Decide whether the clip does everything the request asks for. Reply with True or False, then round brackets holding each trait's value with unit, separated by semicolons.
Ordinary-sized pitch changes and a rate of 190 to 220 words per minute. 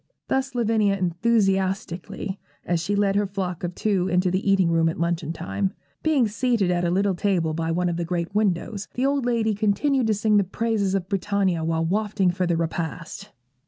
True (3.4 semitones; 195 wpm)